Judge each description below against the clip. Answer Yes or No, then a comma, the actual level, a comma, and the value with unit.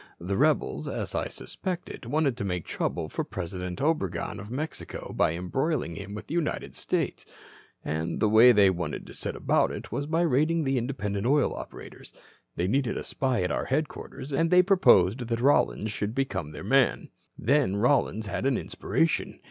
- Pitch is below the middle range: Yes, low, 120 Hz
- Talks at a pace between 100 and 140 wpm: No, average, 180 wpm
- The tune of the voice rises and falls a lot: Yes, wide, 7.0 semitones